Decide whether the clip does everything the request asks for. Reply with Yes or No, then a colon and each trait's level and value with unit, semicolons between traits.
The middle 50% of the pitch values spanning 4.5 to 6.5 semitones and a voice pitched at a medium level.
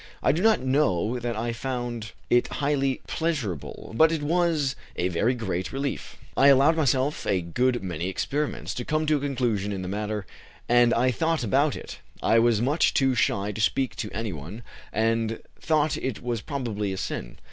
No: average, 4.9 semitones; low, 120 Hz